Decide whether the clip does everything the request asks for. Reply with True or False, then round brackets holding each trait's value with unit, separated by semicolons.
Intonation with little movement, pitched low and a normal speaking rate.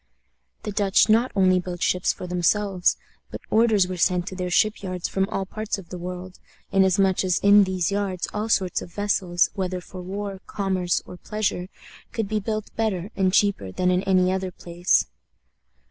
False (2.0 semitones; 190 Hz; 180 wpm)